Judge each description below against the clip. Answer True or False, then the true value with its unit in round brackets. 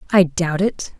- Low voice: False (180 Hz)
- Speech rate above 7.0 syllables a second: False (4.0 syllables/s)